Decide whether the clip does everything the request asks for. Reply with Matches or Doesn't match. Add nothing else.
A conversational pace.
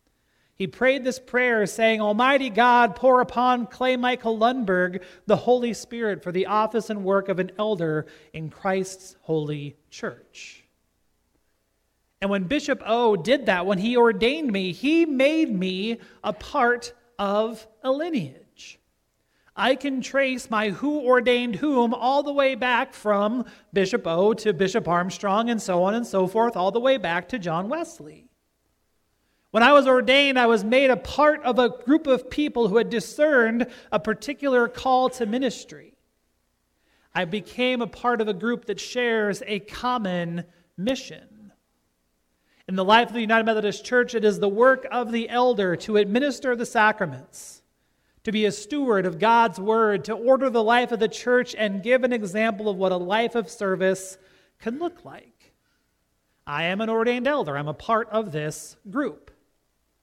Matches